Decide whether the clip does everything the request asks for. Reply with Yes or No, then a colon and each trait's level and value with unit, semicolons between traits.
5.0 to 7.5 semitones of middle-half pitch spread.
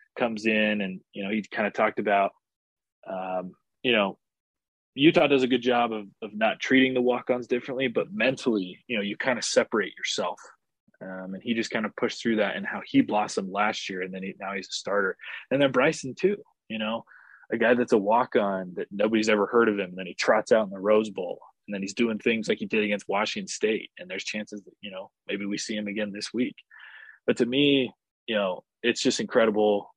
No: average, 3.7 semitones